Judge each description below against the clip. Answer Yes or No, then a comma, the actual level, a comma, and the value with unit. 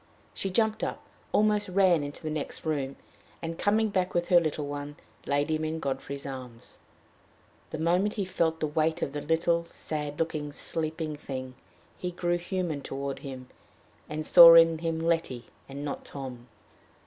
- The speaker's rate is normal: Yes, average, 165 wpm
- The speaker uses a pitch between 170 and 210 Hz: No, medium, 160 Hz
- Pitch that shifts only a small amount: No, average, 3.3 semitones